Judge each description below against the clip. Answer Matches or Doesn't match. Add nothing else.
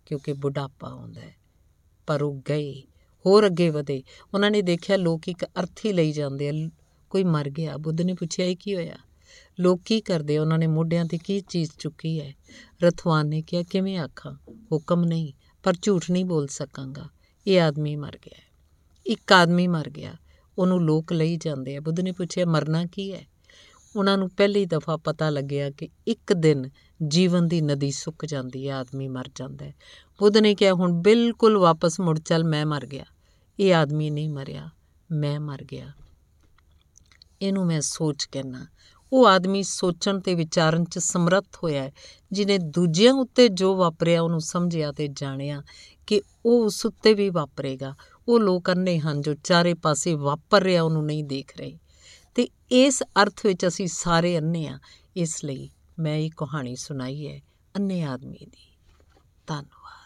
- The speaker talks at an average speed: Doesn't match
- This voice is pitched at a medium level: Matches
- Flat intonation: Doesn't match